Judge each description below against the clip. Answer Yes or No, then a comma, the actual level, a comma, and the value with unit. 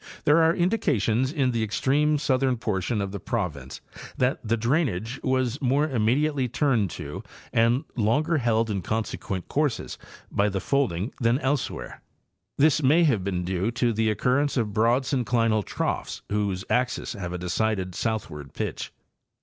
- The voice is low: Yes, low, 115 Hz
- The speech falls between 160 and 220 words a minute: No, average, 150 wpm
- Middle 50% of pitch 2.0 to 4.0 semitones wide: No, average, 5.0 semitones